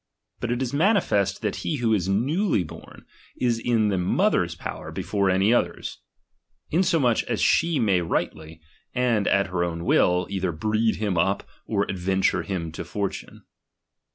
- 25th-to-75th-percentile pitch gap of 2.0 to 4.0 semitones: No, average, 4.6 semitones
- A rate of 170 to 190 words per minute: Yes, average, 175 wpm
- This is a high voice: No, low, 100 Hz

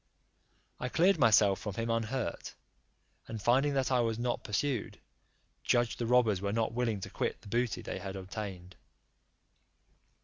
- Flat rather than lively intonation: No, average, 3.4 semitones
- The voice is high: No, low, 115 Hz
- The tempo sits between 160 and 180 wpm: No, average, 150 wpm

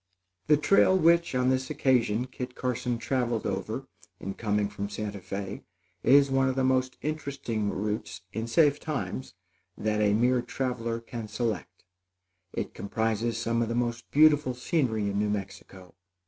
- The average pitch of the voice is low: Yes, low, 120 Hz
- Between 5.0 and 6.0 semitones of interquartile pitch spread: No, average, 3.7 semitones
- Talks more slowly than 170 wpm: Yes, average, 155 wpm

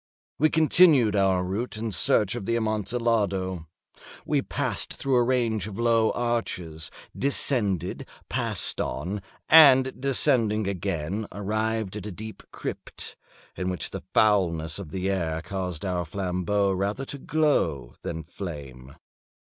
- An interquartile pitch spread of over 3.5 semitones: Yes, average, 4.3 semitones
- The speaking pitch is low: Yes, low, 100 Hz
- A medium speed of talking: No, slow, 130 wpm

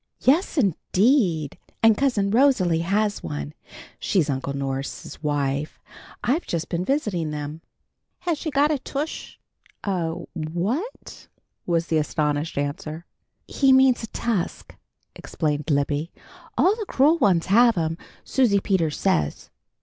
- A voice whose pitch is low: No, medium, 180 Hz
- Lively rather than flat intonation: Yes, wide, 9.0 semitones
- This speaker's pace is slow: Yes, slow, 120 wpm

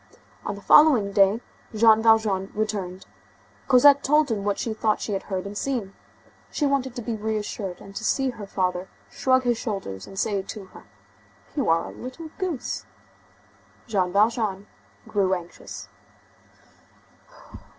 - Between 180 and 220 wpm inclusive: No, average, 150 wpm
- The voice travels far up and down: No, average, 4.0 semitones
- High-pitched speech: Yes, high, 215 Hz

